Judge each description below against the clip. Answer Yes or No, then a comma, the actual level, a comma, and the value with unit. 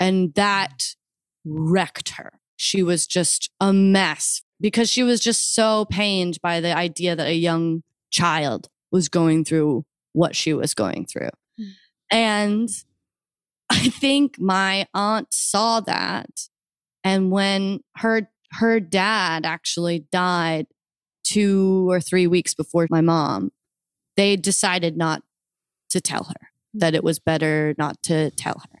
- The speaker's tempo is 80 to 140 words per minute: Yes, slow, 135 wpm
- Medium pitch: Yes, medium, 180 Hz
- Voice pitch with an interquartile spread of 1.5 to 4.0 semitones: Yes, average, 3.7 semitones